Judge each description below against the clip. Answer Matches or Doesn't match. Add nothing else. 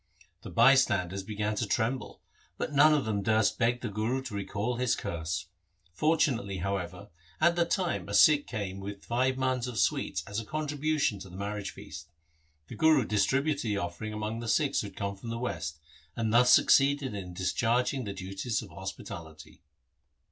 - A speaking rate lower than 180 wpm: Doesn't match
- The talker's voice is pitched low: Matches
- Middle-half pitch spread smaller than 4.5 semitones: Doesn't match